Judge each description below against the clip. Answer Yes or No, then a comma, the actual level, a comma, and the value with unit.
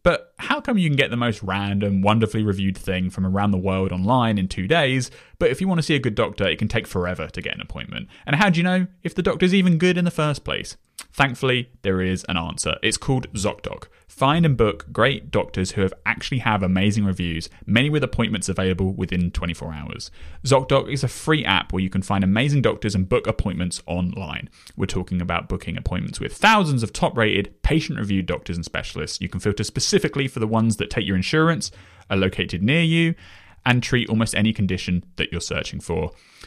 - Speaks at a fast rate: Yes, fast, 215 wpm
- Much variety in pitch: Yes, wide, 6.5 semitones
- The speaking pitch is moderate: No, low, 105 Hz